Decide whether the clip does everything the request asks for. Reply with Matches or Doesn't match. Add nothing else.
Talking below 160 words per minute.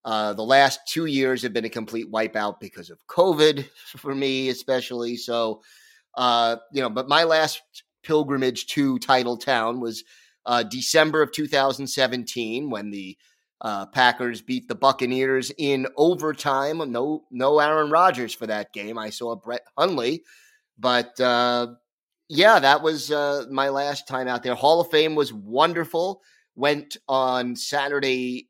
Matches